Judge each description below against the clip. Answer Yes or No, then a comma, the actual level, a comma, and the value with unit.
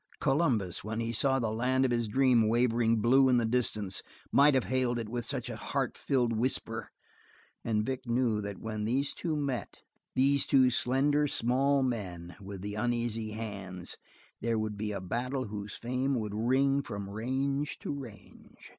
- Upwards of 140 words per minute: Yes, average, 175 wpm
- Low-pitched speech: Yes, low, 120 Hz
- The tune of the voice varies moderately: Yes, average, 3.5 semitones